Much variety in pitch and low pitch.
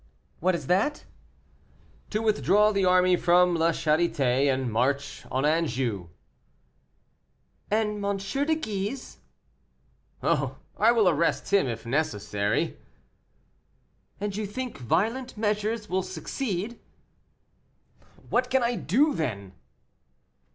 No: wide, 6.5 semitones; medium, 185 Hz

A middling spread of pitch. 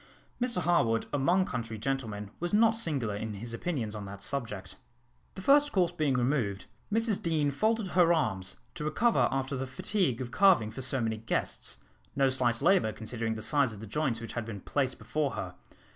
No: wide, 7.5 semitones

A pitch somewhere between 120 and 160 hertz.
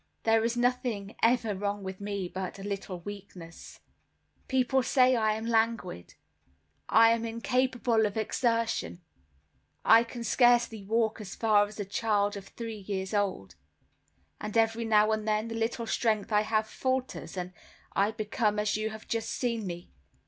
No: high, 220 Hz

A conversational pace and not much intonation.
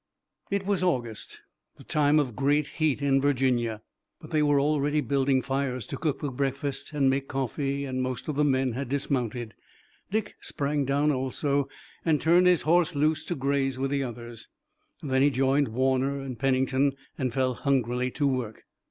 Yes: average, 175 wpm; narrow, 2.1 semitones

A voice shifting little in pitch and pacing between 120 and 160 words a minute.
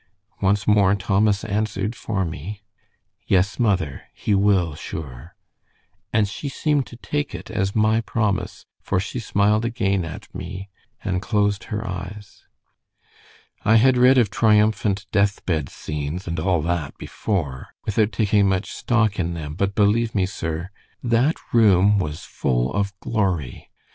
No: average, 3.1 semitones; average, 145 wpm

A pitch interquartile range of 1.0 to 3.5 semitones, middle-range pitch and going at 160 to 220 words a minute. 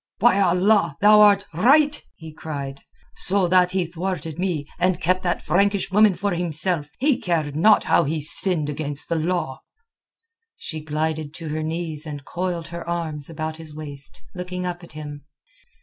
Yes: average, 3.1 semitones; medium, 170 Hz; average, 165 wpm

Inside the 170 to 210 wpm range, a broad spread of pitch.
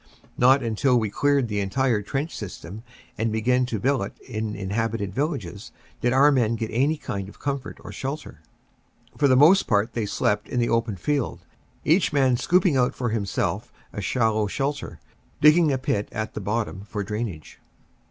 No: average, 175 wpm; average, 4.6 semitones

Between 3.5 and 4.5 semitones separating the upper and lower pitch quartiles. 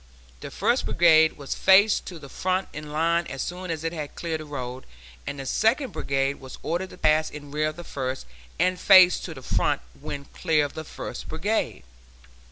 Yes: average, 3.9 semitones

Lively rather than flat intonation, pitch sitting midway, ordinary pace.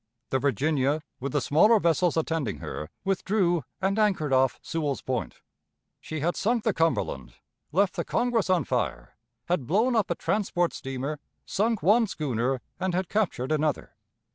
Yes: wide, 6.2 semitones; medium, 165 Hz; average, 155 wpm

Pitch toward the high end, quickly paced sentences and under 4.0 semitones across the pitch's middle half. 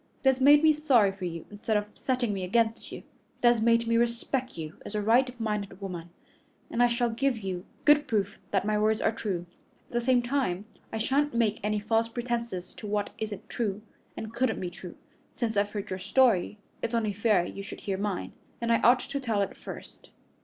Yes: high, 220 Hz; fast, 215 wpm; average, 3.0 semitones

